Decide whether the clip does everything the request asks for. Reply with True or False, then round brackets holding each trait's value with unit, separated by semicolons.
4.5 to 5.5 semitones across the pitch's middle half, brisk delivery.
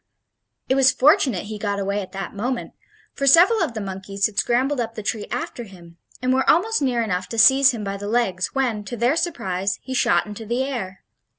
True (4.9 semitones; 215 wpm)